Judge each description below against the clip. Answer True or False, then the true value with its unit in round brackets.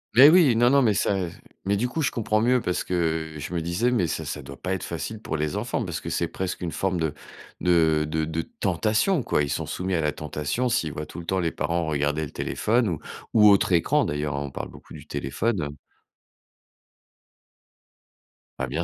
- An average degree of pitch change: False (5.8 semitones)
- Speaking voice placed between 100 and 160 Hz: False (85 Hz)